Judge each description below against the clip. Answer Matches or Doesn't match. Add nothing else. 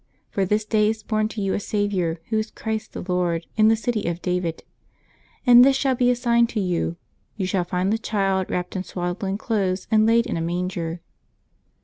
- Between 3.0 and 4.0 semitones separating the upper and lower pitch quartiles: Matches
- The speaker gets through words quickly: Matches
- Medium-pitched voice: Doesn't match